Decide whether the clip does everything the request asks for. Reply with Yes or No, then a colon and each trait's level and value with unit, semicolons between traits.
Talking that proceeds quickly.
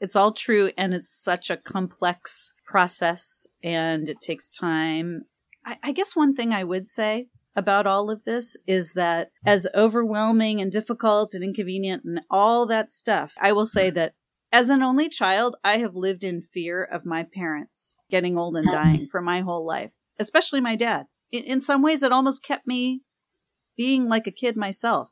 No: average, 185 wpm